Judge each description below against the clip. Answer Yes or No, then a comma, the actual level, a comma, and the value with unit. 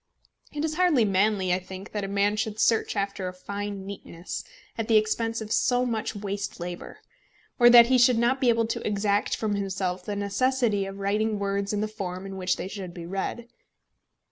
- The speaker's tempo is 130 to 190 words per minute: No, average, 200 wpm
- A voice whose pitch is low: No, high, 205 Hz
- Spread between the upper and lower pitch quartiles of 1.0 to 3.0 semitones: Yes, narrow, 2.6 semitones